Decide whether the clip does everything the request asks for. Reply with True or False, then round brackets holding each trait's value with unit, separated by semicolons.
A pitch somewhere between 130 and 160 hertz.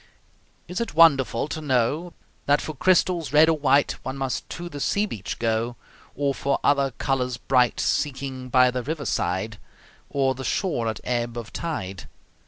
True (135 Hz)